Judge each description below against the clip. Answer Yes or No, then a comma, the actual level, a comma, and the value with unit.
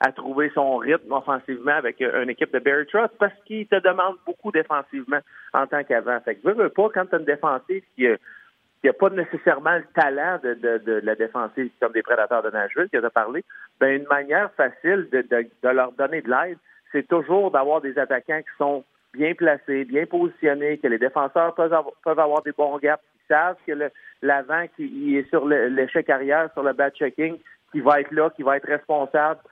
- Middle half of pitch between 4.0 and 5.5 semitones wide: No, average, 3.3 semitones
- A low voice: No, medium, 150 Hz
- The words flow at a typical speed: Yes, average, 210 wpm